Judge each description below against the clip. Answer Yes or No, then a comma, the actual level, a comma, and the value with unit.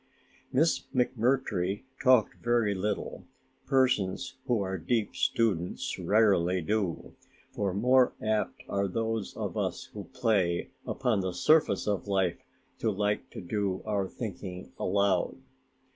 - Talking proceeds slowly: Yes, slow, 125 wpm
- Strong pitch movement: No, average, 3.5 semitones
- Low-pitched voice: Yes, low, 105 Hz